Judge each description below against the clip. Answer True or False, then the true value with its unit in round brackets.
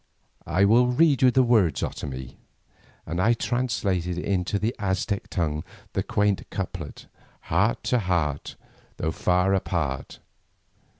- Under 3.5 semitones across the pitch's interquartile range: False (5.0 semitones)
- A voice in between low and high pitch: False (95 Hz)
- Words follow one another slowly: True (125 wpm)